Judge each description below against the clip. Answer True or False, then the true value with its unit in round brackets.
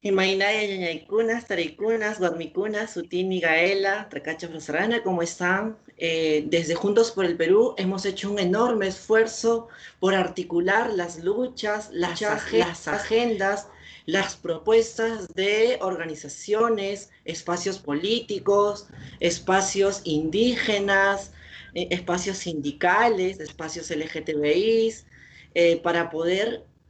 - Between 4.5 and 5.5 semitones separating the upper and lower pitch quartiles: False (3.8 semitones)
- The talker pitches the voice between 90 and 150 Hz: False (190 Hz)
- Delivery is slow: True (105 wpm)